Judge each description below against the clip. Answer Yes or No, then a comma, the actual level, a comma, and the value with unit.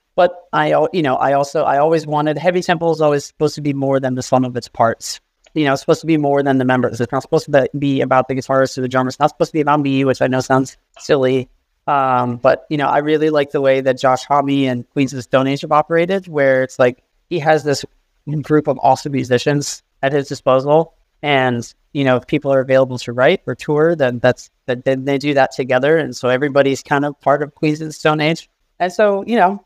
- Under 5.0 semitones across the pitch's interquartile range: Yes, average, 2.7 semitones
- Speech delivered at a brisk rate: Yes, fast, 250 wpm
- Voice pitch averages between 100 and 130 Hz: No, medium, 140 Hz